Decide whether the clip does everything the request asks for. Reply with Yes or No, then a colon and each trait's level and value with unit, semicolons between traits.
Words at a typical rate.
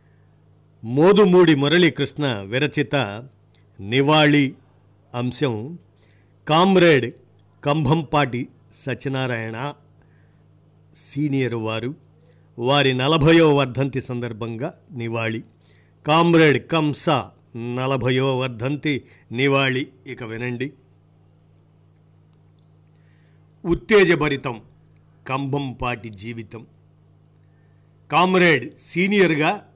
No: slow, 55 wpm